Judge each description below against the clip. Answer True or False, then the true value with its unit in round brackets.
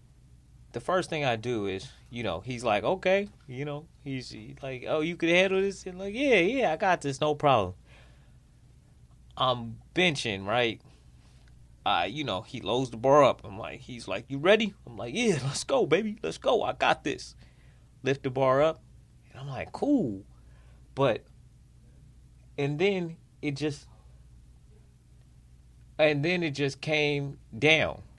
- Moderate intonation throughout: False (5.7 semitones)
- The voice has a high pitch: False (135 Hz)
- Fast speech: False (165 wpm)